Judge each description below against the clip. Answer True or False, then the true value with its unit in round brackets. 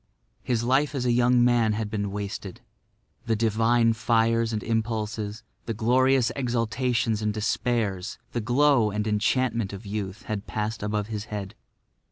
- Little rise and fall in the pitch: True (2.3 semitones)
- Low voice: True (115 Hz)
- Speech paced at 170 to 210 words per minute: False (150 wpm)